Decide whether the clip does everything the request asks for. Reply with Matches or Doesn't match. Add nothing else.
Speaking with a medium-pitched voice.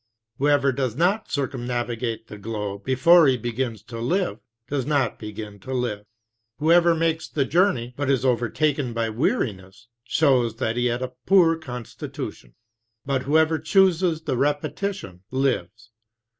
Doesn't match